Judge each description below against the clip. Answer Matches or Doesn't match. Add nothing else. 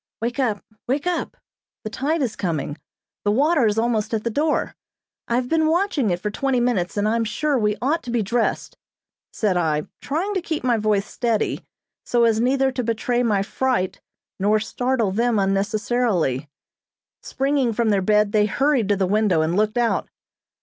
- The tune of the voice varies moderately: Matches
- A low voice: Doesn't match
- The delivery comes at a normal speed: Matches